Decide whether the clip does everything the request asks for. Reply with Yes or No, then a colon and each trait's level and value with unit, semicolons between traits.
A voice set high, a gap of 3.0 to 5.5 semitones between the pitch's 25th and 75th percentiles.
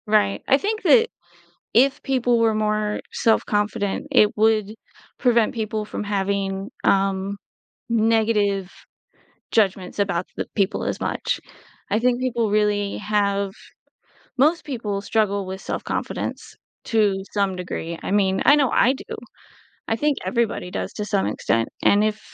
No: high, 210 Hz; narrow, 2.5 semitones